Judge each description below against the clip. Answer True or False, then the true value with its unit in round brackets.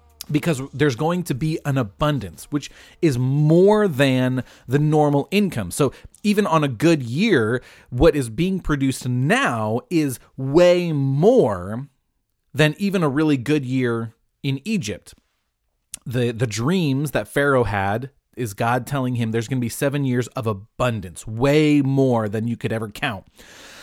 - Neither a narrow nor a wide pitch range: True (4.2 semitones)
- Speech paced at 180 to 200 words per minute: False (155 wpm)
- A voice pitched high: False (135 Hz)